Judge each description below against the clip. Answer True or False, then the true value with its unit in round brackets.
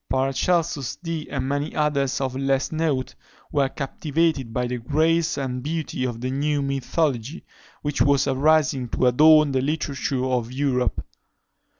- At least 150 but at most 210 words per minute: False (140 wpm)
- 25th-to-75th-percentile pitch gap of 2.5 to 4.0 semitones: True (2.9 semitones)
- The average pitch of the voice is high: False (140 Hz)